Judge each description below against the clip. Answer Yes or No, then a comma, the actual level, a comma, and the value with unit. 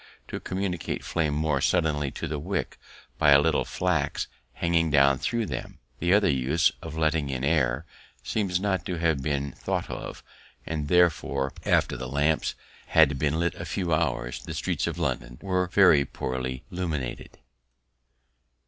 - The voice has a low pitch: Yes, very low, 75 Hz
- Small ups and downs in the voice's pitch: No, average, 3.8 semitones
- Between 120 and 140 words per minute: No, average, 155 wpm